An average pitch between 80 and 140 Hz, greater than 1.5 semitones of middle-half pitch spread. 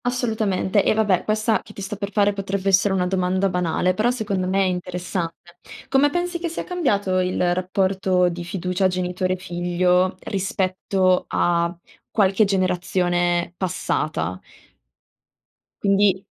No: medium, 185 Hz; narrow, 2.0 semitones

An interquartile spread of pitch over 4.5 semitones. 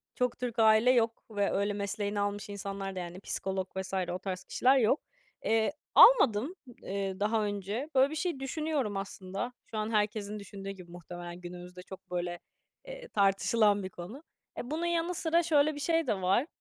Yes: average, 5.1 semitones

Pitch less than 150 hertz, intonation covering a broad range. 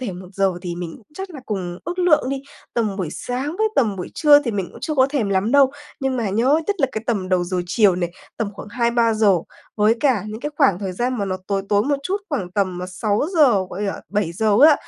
No: high, 215 Hz; wide, 5.8 semitones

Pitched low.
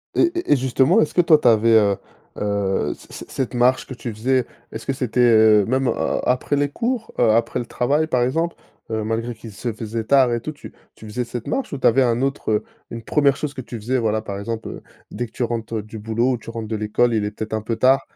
Yes: low, 120 Hz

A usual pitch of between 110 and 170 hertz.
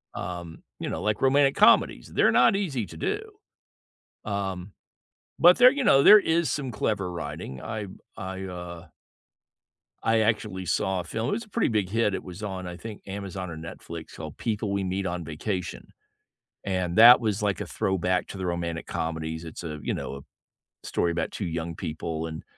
No: very low, 95 Hz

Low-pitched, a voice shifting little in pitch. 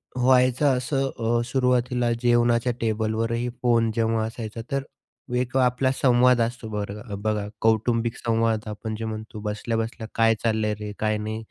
Yes: low, 115 Hz; narrow, 2.0 semitones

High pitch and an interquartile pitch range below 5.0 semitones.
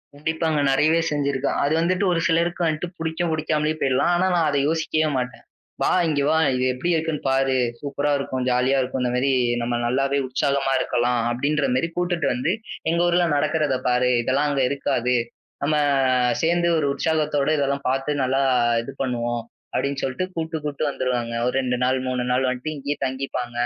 No: medium, 140 Hz; average, 3.5 semitones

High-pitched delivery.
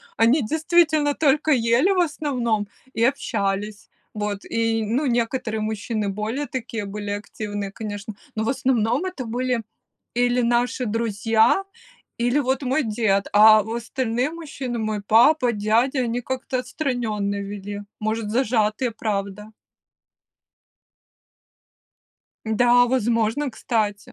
Yes: high, 230 Hz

